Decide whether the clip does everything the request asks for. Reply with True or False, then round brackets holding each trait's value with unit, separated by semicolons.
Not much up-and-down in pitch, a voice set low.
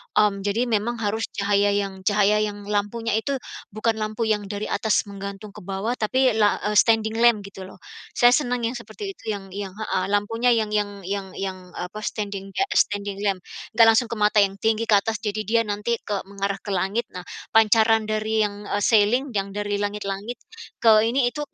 False (1.8 semitones; 210 Hz)